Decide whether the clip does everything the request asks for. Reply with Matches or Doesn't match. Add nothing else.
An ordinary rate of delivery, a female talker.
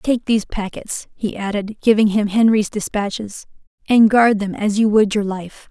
Matches